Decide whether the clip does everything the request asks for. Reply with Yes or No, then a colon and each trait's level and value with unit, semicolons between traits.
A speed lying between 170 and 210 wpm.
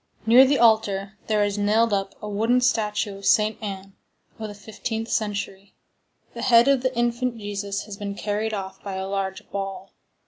Yes: average, 180 wpm